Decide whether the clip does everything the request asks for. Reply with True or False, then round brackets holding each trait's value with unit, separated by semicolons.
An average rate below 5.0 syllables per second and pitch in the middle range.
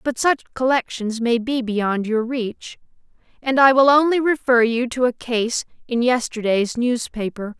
False (4.3 syllables/s; 245 Hz)